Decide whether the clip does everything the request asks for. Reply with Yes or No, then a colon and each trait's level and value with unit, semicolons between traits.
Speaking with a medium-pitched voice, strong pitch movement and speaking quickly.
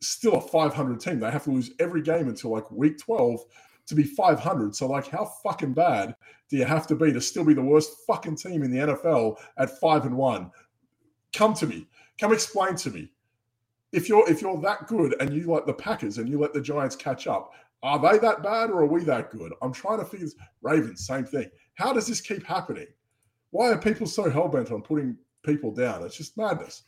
Yes: medium, 150 Hz; wide, 6.2 semitones; fast, 225 wpm